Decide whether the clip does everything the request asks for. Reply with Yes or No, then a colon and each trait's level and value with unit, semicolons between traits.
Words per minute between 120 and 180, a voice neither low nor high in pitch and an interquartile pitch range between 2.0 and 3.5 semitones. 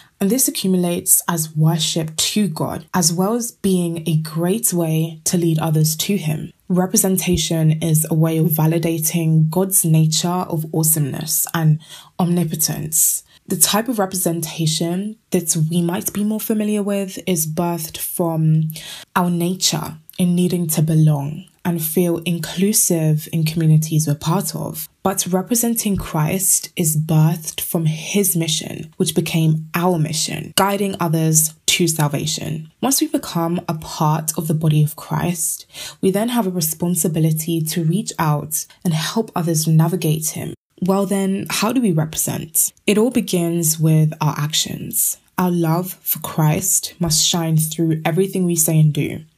Yes: average, 150 wpm; medium, 170 Hz; average, 2.8 semitones